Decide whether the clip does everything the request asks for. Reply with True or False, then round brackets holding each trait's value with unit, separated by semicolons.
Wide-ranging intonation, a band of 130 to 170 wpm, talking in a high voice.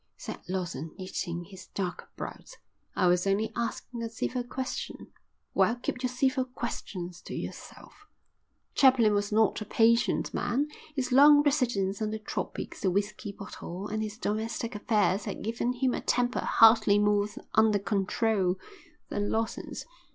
False (3.5 semitones; 150 wpm; 220 Hz)